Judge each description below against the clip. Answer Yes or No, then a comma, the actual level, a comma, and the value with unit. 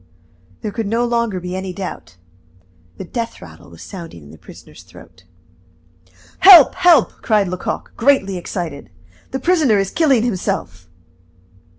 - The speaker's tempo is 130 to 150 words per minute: Yes, average, 140 wpm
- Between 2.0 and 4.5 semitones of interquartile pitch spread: No, average, 5.3 semitones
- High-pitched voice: Yes, high, 200 Hz